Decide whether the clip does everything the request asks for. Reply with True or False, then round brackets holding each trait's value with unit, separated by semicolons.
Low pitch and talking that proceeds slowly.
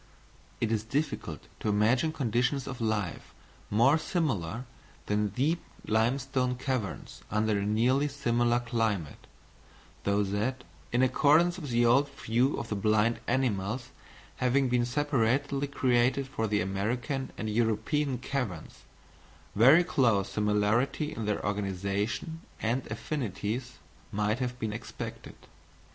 True (120 Hz; 125 wpm)